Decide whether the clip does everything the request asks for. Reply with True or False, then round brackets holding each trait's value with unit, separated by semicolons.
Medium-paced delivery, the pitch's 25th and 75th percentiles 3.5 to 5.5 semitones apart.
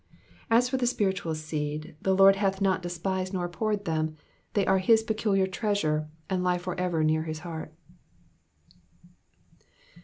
True (150 wpm; 3.8 semitones)